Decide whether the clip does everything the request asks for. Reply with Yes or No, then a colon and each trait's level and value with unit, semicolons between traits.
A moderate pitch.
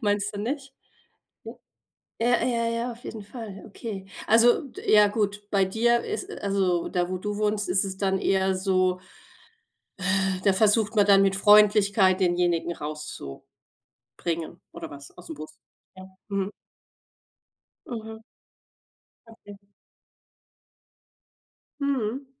No: high, 205 Hz